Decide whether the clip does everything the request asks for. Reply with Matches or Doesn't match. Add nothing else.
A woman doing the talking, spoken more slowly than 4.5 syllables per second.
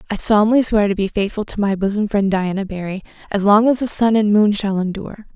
Doesn't match